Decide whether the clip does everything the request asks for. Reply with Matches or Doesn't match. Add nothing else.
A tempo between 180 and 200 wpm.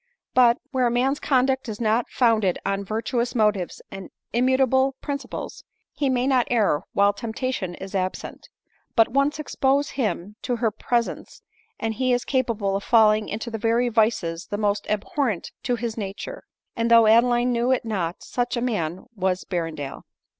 Doesn't match